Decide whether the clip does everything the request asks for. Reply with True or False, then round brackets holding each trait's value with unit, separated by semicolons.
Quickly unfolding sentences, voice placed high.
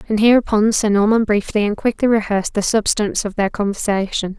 False (180 wpm; 215 Hz)